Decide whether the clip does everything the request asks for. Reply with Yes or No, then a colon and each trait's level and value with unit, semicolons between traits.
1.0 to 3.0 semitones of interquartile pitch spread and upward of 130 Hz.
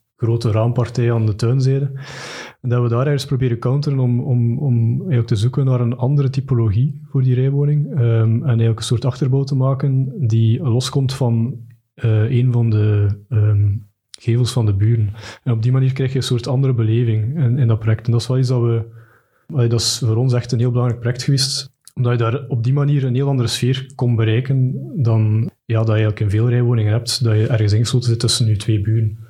No: narrow, 2.5 semitones; low, 120 Hz